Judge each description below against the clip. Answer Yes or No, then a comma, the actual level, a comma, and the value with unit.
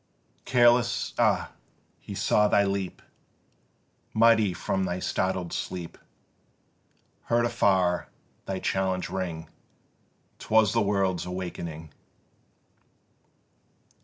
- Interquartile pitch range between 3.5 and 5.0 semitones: No, average, 2.8 semitones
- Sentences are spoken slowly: Yes, slow, 85 wpm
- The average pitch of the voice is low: Yes, very low, 95 Hz